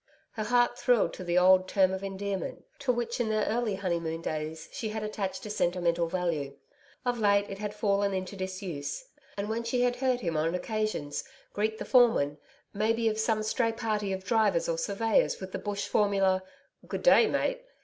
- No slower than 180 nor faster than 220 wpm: Yes, average, 190 wpm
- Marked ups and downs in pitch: No, average, 3.4 semitones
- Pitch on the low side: No, high, 205 Hz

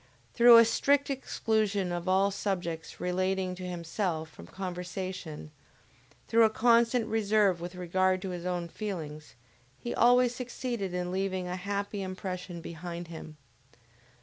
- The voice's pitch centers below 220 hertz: Yes, medium, 185 Hz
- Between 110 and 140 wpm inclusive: Yes, slow, 135 wpm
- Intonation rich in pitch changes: No, average, 3.5 semitones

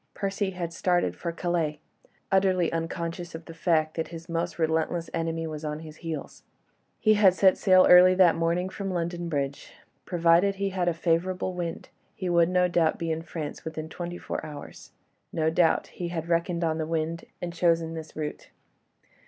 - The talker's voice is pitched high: No, medium, 170 Hz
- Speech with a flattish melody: Yes, narrow, 1.7 semitones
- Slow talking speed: No, average, 180 wpm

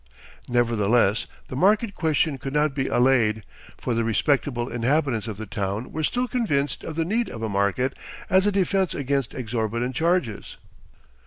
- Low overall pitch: Yes, low, 130 Hz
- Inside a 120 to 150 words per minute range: No, average, 160 wpm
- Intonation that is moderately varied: No, wide, 5.9 semitones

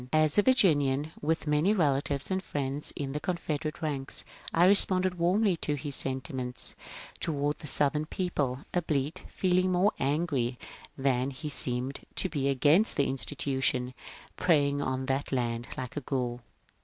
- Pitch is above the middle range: No, medium, 145 Hz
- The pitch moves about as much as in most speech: Yes, average, 4.1 semitones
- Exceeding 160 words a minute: No, average, 150 wpm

